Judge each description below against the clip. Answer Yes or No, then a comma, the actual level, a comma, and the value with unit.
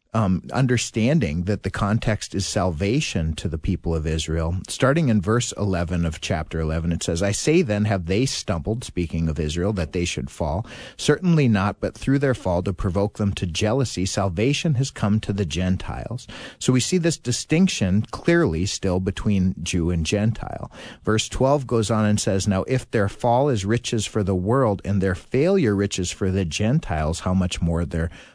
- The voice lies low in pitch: Yes, low, 100 Hz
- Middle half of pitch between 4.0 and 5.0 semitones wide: Yes, average, 4.7 semitones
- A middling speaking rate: Yes, average, 185 wpm